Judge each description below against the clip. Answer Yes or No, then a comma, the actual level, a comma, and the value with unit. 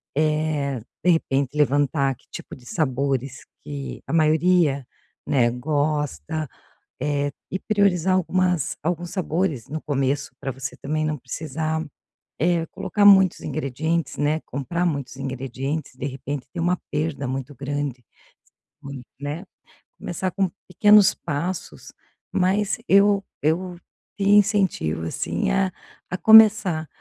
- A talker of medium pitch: Yes, medium, 155 Hz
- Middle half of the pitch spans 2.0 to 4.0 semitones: No, average, 4.6 semitones